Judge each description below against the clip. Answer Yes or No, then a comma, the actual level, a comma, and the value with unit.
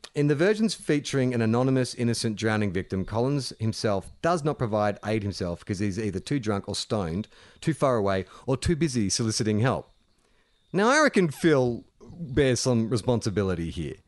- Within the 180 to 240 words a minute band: No, average, 165 wpm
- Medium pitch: No, low, 120 Hz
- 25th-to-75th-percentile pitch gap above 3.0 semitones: Yes, wide, 5.6 semitones